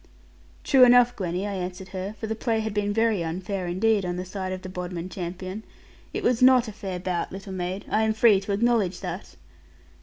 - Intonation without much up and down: No, average, 3.2 semitones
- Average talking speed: No, fast, 210 wpm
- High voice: Yes, high, 195 Hz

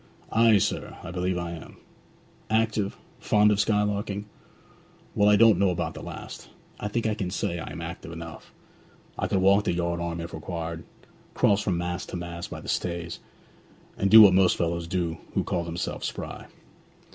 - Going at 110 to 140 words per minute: No, average, 180 wpm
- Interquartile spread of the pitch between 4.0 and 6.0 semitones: No, average, 3.3 semitones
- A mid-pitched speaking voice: No, very low, 90 Hz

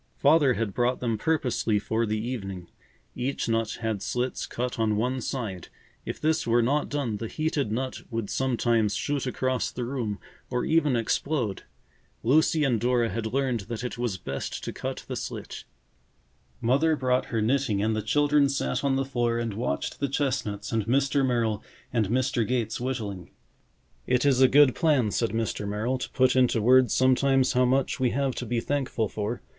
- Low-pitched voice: Yes, low, 125 Hz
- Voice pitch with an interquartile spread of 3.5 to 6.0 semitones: No, average, 3.1 semitones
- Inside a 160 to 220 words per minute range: Yes, average, 180 wpm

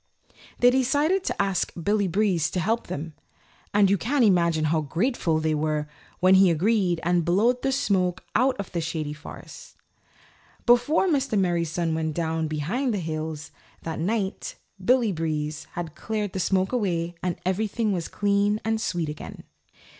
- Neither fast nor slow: Yes, average, 165 wpm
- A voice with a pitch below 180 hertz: No, medium, 185 Hz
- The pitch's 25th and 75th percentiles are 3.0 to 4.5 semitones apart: No, average, 5.2 semitones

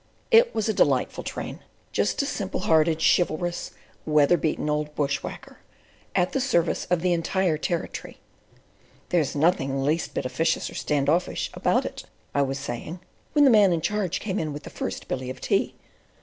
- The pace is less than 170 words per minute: No, average, 175 wpm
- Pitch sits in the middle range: Yes, medium, 165 Hz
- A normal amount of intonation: Yes, average, 3.7 semitones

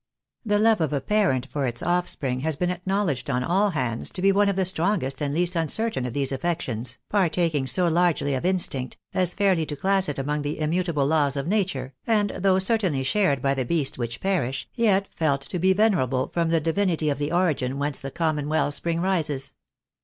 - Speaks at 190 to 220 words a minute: Yes, fast, 205 wpm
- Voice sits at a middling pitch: Yes, medium, 160 Hz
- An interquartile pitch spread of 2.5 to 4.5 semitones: No, average, 5.3 semitones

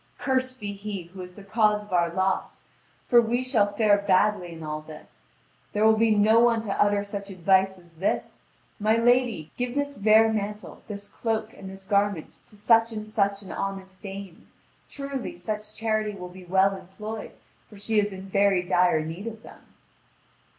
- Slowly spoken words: No, average, 185 wpm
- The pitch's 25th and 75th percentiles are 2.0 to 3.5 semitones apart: Yes, narrow, 2.5 semitones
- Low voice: No, high, 205 Hz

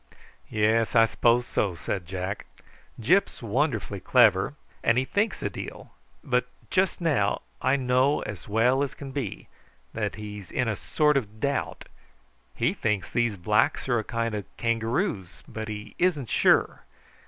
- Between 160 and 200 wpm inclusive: No, average, 150 wpm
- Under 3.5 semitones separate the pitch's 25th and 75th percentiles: No, average, 4.2 semitones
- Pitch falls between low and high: No, low, 115 Hz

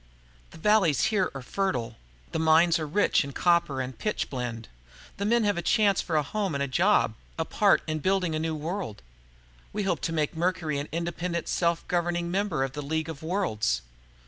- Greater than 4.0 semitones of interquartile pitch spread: Yes, average, 4.6 semitones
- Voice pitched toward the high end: No, medium, 165 Hz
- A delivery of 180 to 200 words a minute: Yes, average, 195 wpm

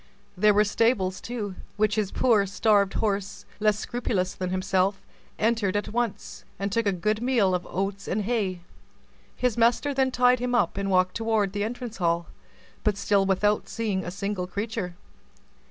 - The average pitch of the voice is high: Yes, high, 205 Hz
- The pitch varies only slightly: No, average, 3.0 semitones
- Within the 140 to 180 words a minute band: Yes, average, 170 wpm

